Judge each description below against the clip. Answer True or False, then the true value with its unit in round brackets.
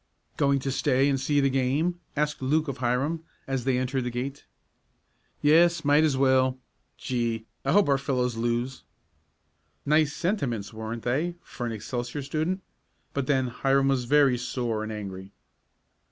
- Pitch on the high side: False (135 Hz)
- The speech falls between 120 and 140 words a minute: False (160 wpm)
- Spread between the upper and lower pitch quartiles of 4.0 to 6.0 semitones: False (3.1 semitones)